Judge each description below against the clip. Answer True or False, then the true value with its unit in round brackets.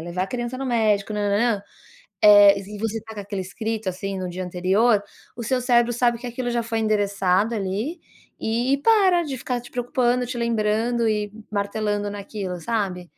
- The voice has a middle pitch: False (215 Hz)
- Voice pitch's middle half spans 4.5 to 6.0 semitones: False (3.2 semitones)